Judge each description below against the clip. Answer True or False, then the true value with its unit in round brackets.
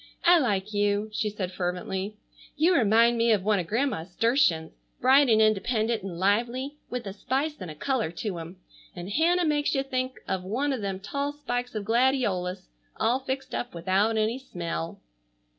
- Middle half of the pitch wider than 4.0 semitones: True (5.4 semitones)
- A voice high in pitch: True (220 Hz)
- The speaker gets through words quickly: False (175 wpm)